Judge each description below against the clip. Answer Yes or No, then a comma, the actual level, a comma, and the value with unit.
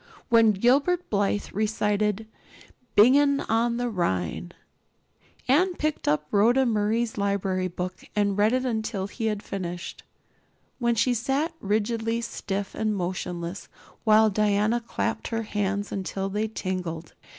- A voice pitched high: Yes, high, 210 Hz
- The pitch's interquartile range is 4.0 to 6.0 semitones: No, average, 3.3 semitones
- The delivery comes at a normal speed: No, slow, 130 wpm